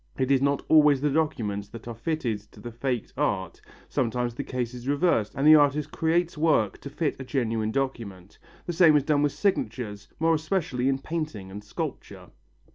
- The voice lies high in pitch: No, low, 135 Hz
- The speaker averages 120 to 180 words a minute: No, average, 190 wpm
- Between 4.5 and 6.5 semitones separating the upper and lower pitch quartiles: Yes, average, 4.9 semitones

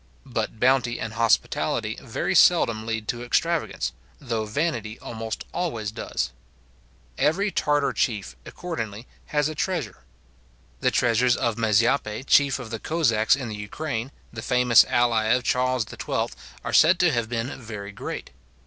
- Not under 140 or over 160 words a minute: Yes, average, 145 wpm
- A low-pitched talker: Yes, low, 120 Hz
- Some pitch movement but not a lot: Yes, average, 4.0 semitones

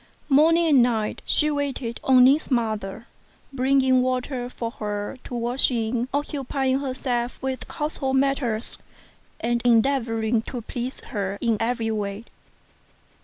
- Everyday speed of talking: No, slow, 130 wpm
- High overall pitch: Yes, very high, 250 Hz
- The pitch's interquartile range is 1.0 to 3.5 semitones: Yes, average, 2.9 semitones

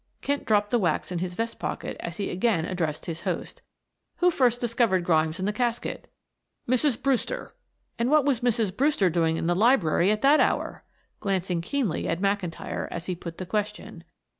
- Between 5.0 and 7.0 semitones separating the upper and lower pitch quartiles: Yes, wide, 5.6 semitones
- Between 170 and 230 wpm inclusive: Yes, average, 185 wpm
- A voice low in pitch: No, high, 205 Hz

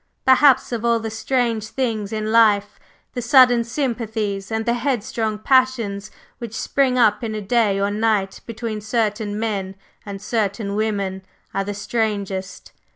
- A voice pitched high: Yes, high, 220 Hz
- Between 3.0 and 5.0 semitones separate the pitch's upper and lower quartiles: No, narrow, 2.5 semitones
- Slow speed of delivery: No, average, 155 wpm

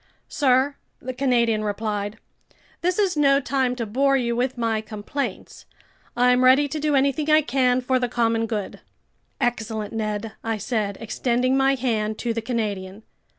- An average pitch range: Yes, average, 3.5 semitones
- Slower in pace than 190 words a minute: Yes, average, 155 wpm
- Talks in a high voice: Yes, high, 245 Hz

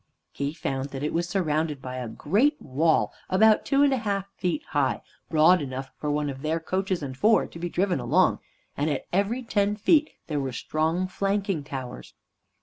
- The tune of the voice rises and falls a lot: Yes, wide, 5.8 semitones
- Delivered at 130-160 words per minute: No, average, 190 wpm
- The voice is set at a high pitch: No, medium, 165 Hz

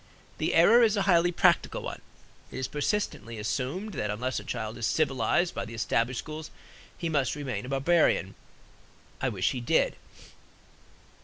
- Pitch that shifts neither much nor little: No, wide, 6.6 semitones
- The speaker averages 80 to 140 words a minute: No, average, 160 wpm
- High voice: No, low, 135 Hz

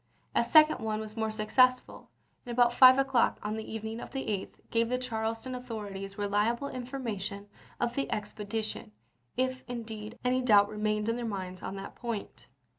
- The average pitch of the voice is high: Yes, high, 225 Hz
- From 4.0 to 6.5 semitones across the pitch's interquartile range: No, average, 3.0 semitones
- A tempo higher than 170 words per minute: Yes, average, 190 wpm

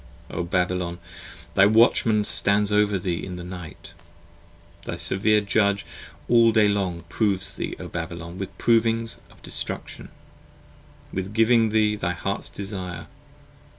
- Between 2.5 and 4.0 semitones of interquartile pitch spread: Yes, average, 3.1 semitones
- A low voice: Yes, low, 100 Hz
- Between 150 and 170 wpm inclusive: No, slow, 135 wpm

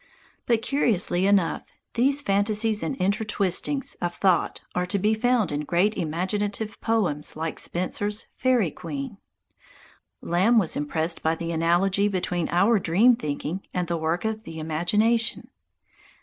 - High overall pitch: Yes, high, 195 Hz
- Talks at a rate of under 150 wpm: Yes, average, 140 wpm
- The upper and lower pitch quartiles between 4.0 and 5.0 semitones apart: Yes, average, 4.3 semitones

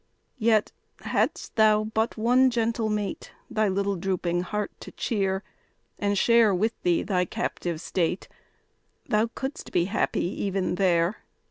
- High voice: Yes, high, 205 Hz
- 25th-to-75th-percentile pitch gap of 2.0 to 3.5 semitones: Yes, average, 3.1 semitones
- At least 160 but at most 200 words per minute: No, slow, 135 wpm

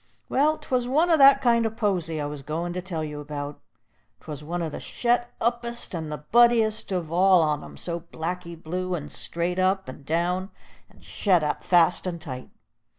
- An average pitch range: No, wide, 6.0 semitones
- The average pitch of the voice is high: No, medium, 175 Hz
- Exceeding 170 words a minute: Yes, average, 195 wpm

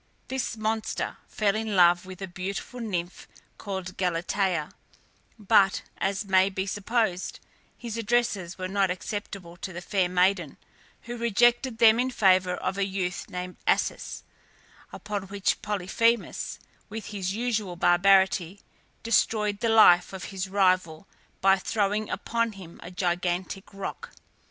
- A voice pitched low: No, high, 195 Hz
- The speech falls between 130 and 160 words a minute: Yes, slow, 135 wpm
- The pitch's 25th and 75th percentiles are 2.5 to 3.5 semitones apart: Yes, average, 2.9 semitones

